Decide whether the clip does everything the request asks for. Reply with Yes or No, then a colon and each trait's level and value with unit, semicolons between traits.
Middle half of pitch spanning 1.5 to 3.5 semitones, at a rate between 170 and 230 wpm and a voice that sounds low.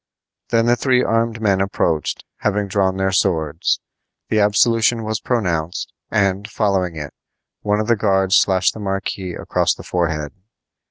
No: average, 2.9 semitones; average, 150 wpm; low, 100 Hz